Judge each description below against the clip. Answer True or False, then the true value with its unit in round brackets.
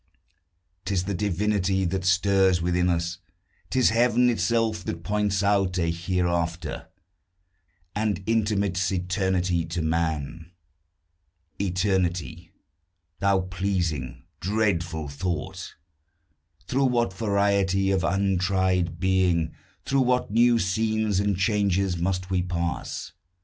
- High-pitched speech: False (95 Hz)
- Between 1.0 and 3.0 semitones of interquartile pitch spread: True (2.7 semitones)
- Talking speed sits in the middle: False (100 wpm)